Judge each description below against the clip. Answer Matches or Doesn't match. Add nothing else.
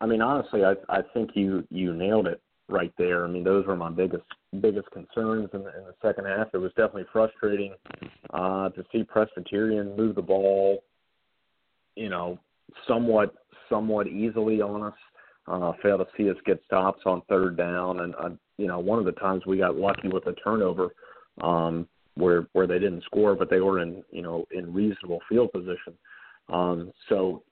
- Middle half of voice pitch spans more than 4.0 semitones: Doesn't match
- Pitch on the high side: Doesn't match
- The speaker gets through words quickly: Doesn't match